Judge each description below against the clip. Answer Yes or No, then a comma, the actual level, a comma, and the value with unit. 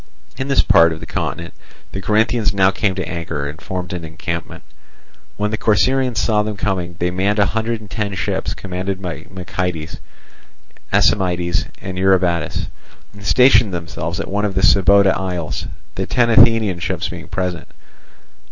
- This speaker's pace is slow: No, average, 160 wpm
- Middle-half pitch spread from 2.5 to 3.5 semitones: Yes, average, 3.2 semitones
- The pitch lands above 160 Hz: No, very low, 95 Hz